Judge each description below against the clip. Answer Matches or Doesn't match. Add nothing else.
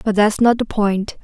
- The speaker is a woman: Matches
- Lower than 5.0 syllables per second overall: Matches